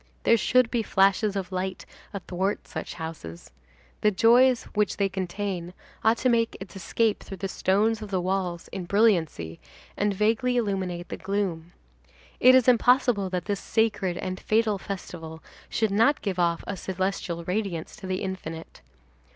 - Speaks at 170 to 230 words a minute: No, average, 160 wpm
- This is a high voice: Yes, high, 195 Hz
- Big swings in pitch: No, average, 3.3 semitones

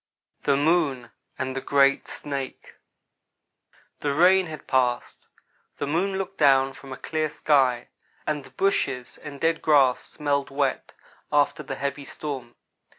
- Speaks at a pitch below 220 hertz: Yes, medium, 140 Hz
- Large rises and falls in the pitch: No, narrow, 2.5 semitones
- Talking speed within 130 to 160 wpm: Yes, average, 140 wpm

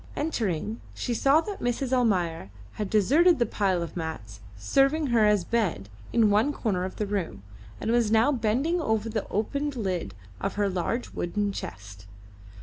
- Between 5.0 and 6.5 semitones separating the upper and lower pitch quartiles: Yes, average, 5.3 semitones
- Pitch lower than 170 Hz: No, high, 215 Hz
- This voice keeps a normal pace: Yes, average, 165 wpm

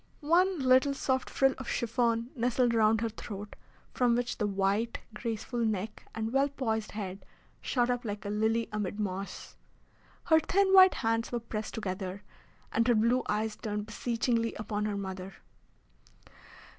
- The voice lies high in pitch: Yes, high, 225 Hz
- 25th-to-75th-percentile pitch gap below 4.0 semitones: Yes, average, 2.8 semitones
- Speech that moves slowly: No, average, 155 wpm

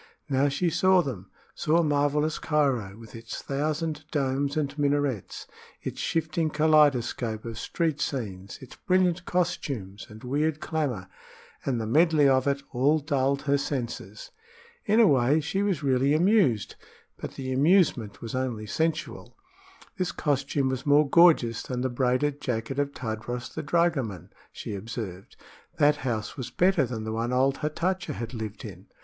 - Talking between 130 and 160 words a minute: Yes, average, 155 wpm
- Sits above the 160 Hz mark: No, medium, 140 Hz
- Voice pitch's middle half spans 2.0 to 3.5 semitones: No, average, 4.4 semitones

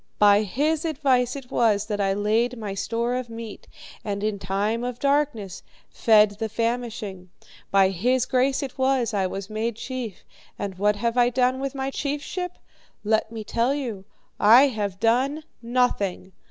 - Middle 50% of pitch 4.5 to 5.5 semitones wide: No, average, 3.8 semitones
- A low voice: No, high, 230 Hz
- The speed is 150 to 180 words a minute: Yes, average, 165 wpm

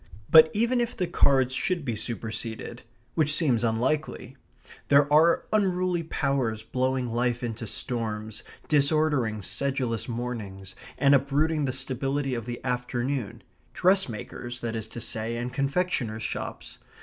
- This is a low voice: Yes, low, 130 Hz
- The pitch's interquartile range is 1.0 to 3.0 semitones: No, average, 4.3 semitones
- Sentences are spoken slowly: Yes, slow, 130 wpm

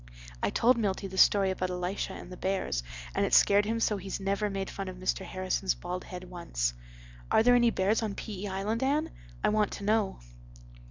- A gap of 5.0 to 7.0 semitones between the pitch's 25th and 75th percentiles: No, narrow, 2.4 semitones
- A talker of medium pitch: No, high, 195 Hz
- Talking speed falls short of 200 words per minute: No, fast, 205 wpm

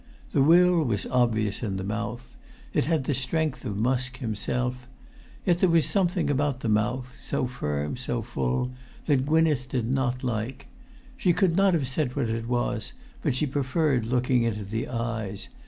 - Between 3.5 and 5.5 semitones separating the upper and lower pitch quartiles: Yes, average, 4.0 semitones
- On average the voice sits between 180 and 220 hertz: No, low, 125 Hz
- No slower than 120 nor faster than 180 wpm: Yes, average, 160 wpm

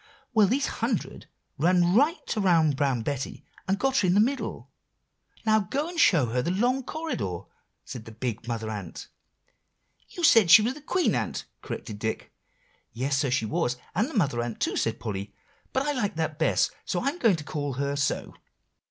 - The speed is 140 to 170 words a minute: No, average, 185 wpm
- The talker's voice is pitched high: No, medium, 165 Hz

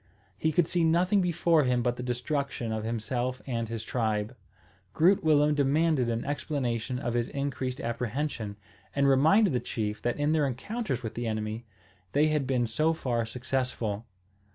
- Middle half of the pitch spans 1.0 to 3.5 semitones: No, average, 4.4 semitones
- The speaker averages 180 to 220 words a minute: No, average, 165 wpm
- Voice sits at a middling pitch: No, low, 130 Hz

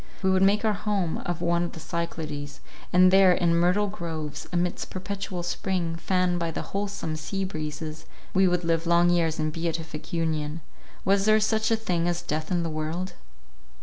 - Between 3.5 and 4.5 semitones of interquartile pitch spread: No, average, 2.7 semitones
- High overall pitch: No, medium, 175 Hz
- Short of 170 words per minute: No, average, 175 wpm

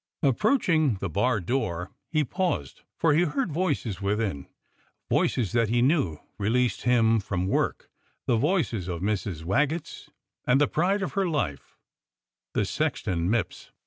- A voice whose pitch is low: Yes, low, 120 Hz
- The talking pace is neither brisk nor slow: Yes, average, 145 wpm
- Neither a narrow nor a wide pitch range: No, wide, 7.7 semitones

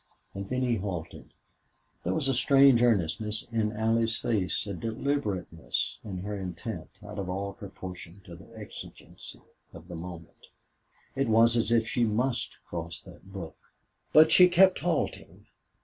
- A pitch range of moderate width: Yes, average, 4.4 semitones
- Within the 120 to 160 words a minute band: Yes, average, 150 wpm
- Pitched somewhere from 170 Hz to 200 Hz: No, low, 105 Hz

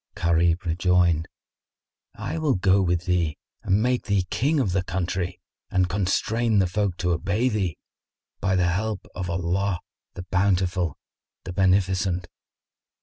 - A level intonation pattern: Yes, narrow, 2.1 semitones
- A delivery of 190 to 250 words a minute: No, average, 140 wpm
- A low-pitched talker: Yes, very low, 95 Hz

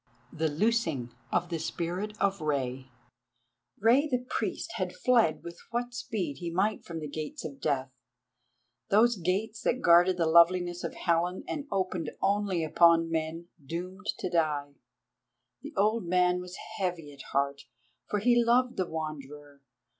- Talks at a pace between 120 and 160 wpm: Yes, average, 150 wpm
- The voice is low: No, medium, 175 Hz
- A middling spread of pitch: Yes, average, 4.6 semitones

